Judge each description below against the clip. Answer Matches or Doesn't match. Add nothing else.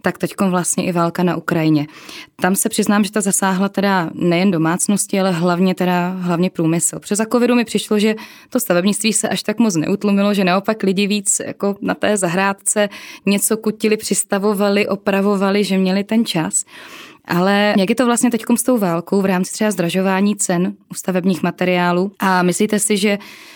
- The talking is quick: Matches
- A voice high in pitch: Matches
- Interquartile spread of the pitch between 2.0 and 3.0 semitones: Matches